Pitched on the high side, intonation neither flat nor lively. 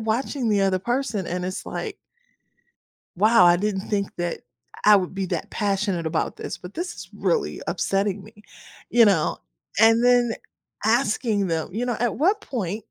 Yes: high, 210 Hz; average, 3.9 semitones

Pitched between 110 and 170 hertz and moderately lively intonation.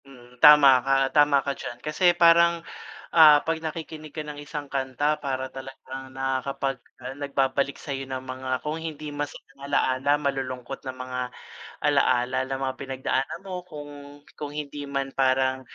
No: medium, 140 Hz; narrow, 2.1 semitones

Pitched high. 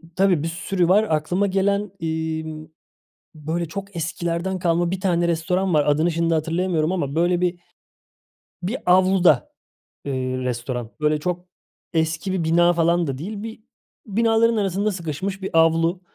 No: medium, 170 Hz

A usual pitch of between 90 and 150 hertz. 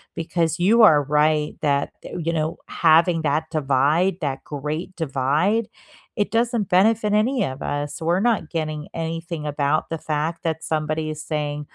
No: medium, 160 Hz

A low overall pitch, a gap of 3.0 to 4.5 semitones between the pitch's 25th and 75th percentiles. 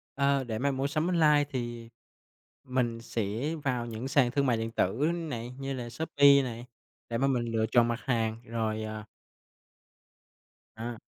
Yes: low, 120 Hz; average, 3.3 semitones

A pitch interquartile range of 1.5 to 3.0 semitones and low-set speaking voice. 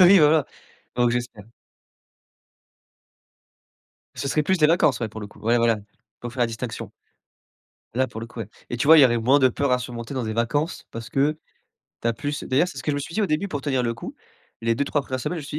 No: average, 4.1 semitones; low, 130 Hz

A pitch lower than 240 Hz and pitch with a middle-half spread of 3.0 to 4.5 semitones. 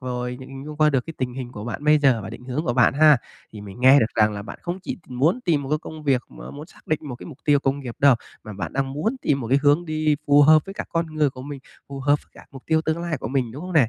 Yes: medium, 140 Hz; average, 3.6 semitones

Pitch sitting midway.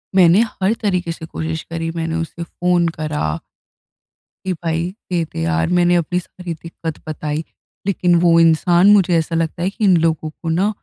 Yes: medium, 170 Hz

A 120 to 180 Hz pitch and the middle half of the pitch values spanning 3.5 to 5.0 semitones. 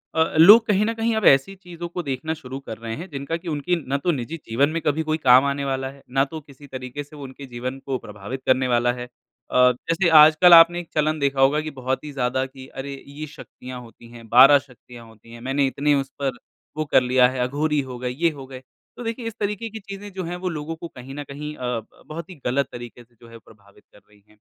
Yes: medium, 140 Hz; average, 4.2 semitones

